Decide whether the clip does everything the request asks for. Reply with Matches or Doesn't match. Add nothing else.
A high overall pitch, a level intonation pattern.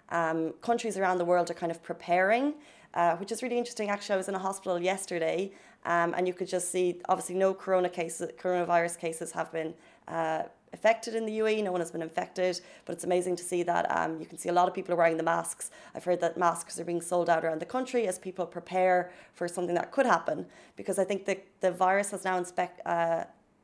Doesn't match